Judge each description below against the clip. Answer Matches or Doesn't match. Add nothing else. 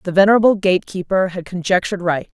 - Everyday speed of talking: Matches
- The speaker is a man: Doesn't match